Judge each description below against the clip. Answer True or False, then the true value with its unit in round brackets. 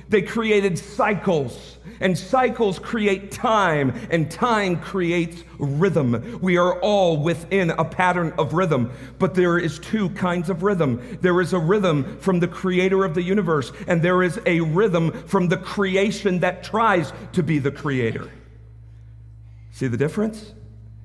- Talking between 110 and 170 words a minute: True (150 wpm)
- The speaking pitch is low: False (180 Hz)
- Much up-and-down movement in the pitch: False (4.3 semitones)